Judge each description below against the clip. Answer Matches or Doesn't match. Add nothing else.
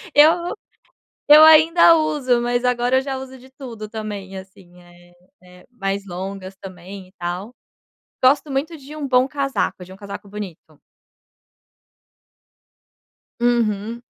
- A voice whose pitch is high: Matches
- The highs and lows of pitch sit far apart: Matches